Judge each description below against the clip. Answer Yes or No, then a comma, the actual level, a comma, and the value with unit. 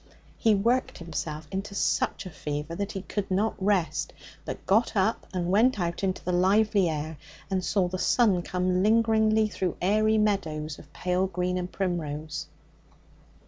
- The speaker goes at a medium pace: Yes, average, 160 wpm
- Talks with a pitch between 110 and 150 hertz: No, medium, 185 Hz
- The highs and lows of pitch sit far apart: No, average, 3.3 semitones